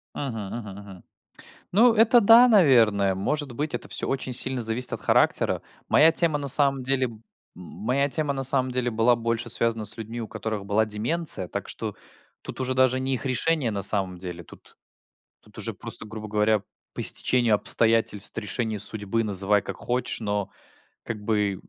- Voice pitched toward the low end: Yes, low, 115 Hz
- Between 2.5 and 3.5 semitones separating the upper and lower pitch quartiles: No, average, 4.3 semitones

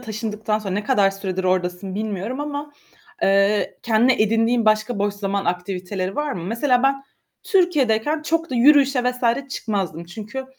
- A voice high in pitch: Yes, high, 220 Hz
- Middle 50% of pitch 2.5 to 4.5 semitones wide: No, average, 5.0 semitones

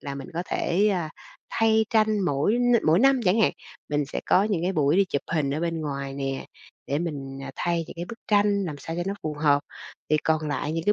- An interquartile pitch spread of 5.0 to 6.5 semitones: Yes, wide, 5.6 semitones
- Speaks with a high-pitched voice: No, medium, 165 Hz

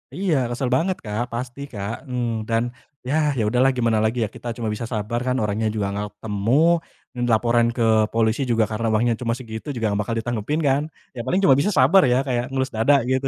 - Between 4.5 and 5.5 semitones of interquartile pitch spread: No, average, 2.8 semitones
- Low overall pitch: Yes, low, 120 Hz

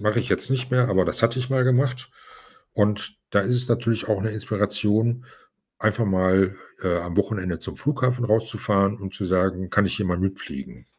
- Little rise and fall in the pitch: No, average, 4.3 semitones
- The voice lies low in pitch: Yes, low, 105 Hz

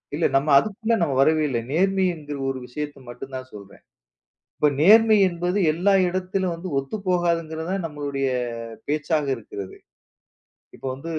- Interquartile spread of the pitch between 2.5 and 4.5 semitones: No, average, 5.0 semitones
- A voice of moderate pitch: Yes, medium, 160 Hz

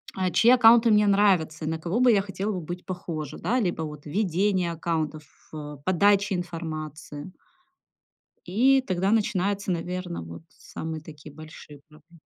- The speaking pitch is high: No, medium, 175 Hz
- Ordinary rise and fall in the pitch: Yes, average, 4.3 semitones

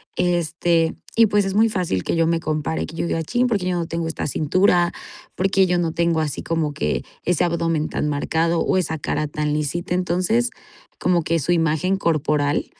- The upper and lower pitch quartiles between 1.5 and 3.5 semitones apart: Yes, narrow, 2.6 semitones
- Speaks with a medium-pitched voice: Yes, medium, 170 Hz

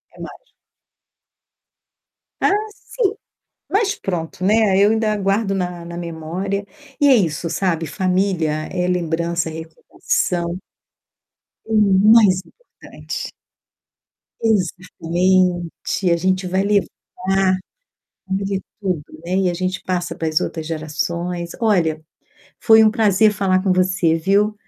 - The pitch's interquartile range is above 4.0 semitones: No, average, 2.8 semitones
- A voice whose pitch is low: No, medium, 185 Hz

